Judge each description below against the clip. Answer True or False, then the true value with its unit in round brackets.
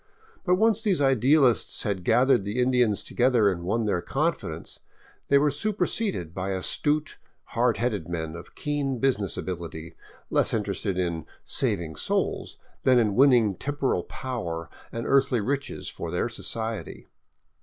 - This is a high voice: False (115 Hz)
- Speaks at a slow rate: False (145 wpm)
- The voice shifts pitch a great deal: True (6.7 semitones)